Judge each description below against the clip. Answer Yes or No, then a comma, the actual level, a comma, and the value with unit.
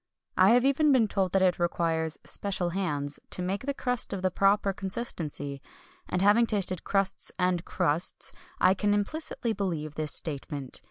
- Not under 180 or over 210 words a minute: No, average, 165 wpm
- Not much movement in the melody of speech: No, average, 3.7 semitones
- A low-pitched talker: No, high, 190 Hz